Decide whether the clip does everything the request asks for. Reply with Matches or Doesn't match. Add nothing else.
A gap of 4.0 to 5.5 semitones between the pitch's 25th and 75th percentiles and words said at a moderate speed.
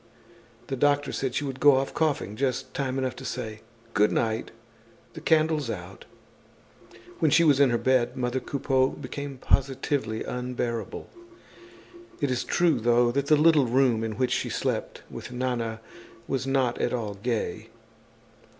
Doesn't match